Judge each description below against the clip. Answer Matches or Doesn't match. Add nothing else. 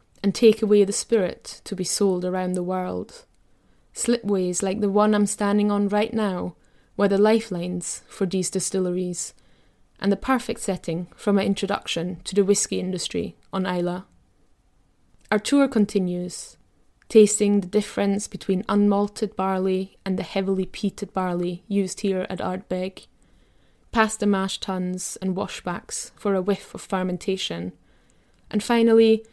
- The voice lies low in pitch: Doesn't match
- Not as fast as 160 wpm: Matches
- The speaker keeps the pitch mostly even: Matches